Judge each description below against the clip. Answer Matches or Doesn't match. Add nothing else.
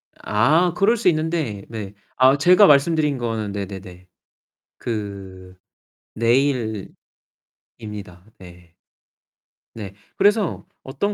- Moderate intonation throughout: Doesn't match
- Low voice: Matches